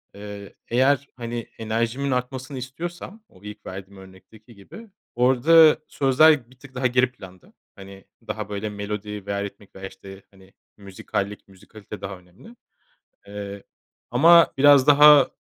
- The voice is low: Yes, low, 110 Hz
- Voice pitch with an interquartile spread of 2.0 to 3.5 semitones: No, average, 5.0 semitones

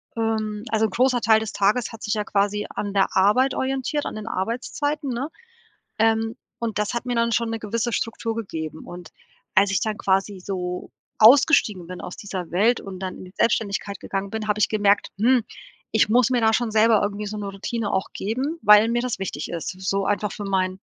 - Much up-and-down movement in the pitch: No, average, 2.8 semitones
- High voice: Yes, high, 215 Hz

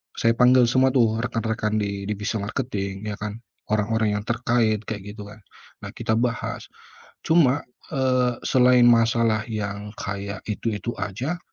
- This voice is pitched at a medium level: No, low, 110 Hz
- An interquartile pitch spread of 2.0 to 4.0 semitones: Yes, average, 2.8 semitones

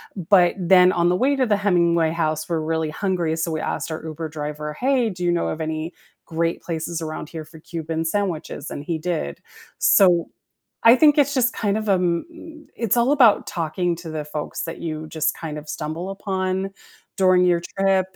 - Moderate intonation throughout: Yes, average, 3.5 semitones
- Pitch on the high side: No, medium, 170 Hz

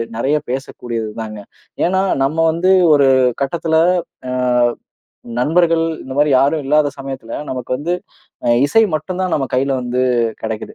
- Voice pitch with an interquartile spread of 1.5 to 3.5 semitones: No, average, 4.3 semitones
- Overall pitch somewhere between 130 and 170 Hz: Yes, medium, 140 Hz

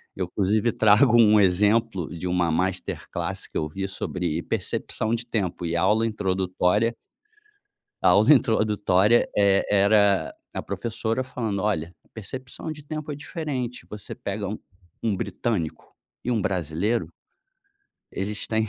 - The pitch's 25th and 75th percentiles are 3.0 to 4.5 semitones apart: Yes, average, 3.6 semitones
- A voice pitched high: No, low, 105 Hz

